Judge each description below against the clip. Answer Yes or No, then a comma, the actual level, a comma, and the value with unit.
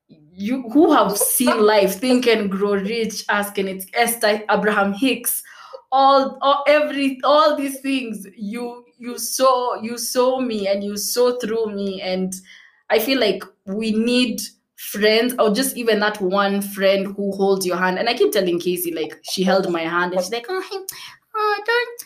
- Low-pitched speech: No, high, 220 Hz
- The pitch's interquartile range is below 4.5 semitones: No, average, 4.8 semitones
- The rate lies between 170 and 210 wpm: Yes, average, 175 wpm